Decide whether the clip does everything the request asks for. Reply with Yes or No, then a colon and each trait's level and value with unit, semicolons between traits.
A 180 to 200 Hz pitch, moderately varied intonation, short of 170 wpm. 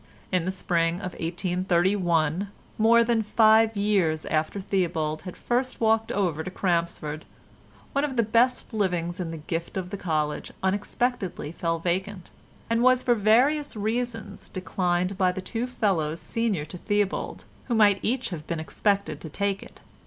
Yes: high, 190 Hz; average, 4.5 semitones; average, 160 wpm